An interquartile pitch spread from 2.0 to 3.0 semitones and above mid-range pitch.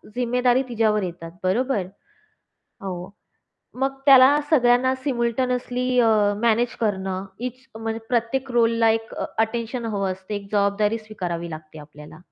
No: average, 4.1 semitones; high, 225 Hz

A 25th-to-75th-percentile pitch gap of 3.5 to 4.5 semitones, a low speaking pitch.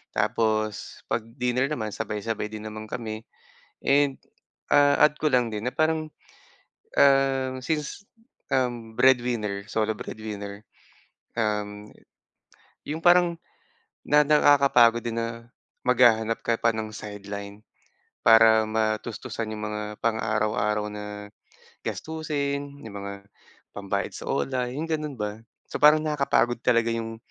Yes: average, 4.1 semitones; low, 115 Hz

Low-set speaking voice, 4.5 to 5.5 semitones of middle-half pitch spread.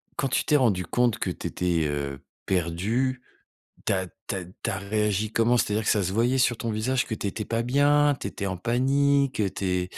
Yes: low, 110 Hz; average, 5.2 semitones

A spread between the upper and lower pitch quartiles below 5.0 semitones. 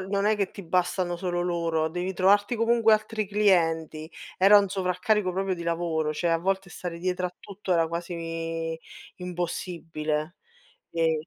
Yes: average, 2.7 semitones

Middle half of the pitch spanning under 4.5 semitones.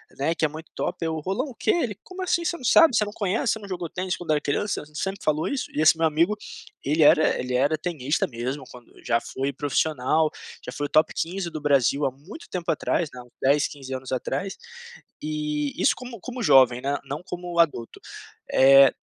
No: average, 5.0 semitones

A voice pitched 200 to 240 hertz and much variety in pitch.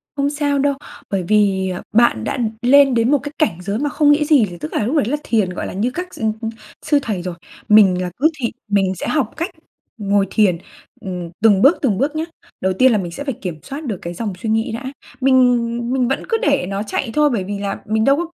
Yes: high, 225 Hz; wide, 6.2 semitones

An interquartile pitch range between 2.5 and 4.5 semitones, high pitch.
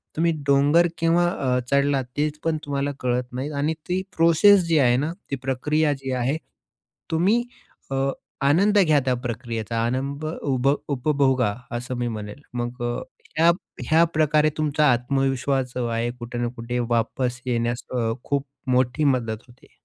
No: average, 3.8 semitones; low, 135 Hz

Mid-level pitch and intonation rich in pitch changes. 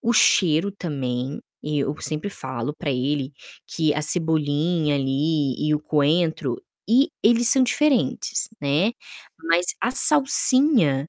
Yes: medium, 155 Hz; wide, 6.2 semitones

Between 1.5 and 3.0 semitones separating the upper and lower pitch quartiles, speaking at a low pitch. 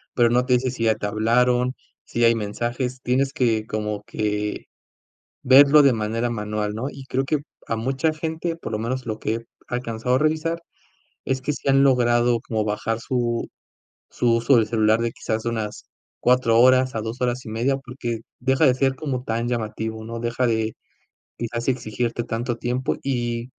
Yes: narrow, 2.5 semitones; low, 120 Hz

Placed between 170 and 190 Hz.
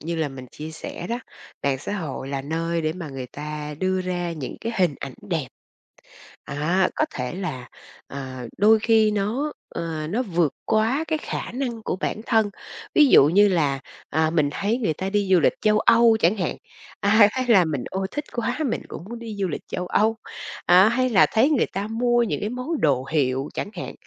Yes: medium, 185 Hz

